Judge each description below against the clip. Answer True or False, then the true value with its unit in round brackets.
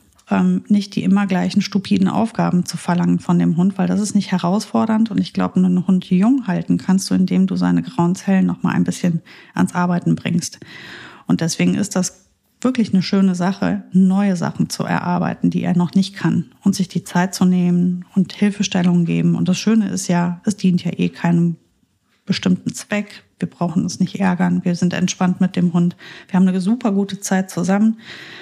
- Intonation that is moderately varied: False (2.1 semitones)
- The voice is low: False (185 Hz)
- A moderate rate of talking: False (195 wpm)